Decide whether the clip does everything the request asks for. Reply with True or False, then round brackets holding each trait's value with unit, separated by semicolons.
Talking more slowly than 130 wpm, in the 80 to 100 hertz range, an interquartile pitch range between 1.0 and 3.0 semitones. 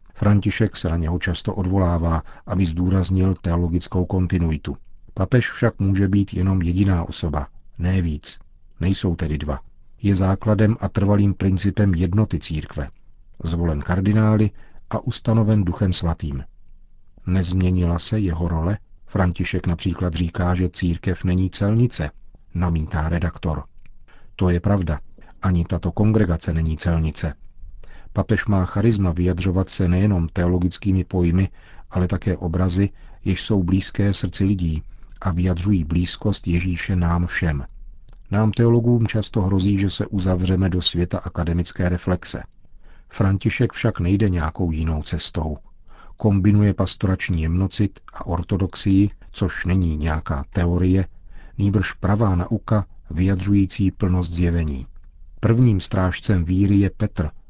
True (120 wpm; 90 Hz; 2.7 semitones)